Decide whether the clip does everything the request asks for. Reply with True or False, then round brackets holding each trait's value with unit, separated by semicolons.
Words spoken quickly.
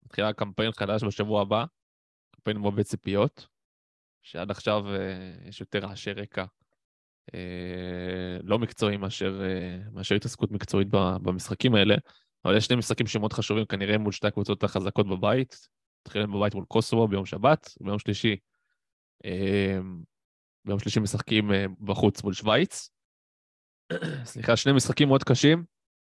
False (130 wpm)